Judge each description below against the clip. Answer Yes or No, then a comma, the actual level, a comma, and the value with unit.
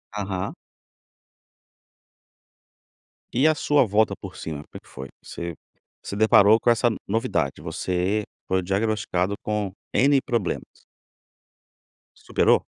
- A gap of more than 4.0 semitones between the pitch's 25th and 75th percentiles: No, average, 3.7 semitones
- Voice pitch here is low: Yes, low, 100 Hz